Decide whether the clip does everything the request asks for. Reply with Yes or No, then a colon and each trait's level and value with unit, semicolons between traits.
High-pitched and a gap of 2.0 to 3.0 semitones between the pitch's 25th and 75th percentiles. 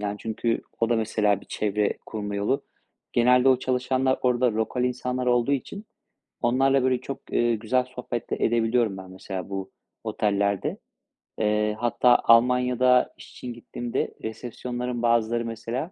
No: low, 120 Hz; narrow, 2.6 semitones